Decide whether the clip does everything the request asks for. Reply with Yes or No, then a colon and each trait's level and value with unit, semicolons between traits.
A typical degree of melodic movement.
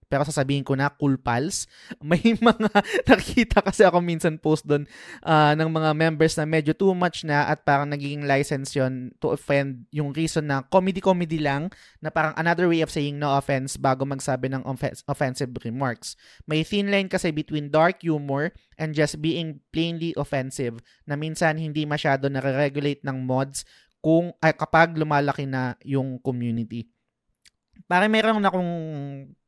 Yes: average, 3.0 semitones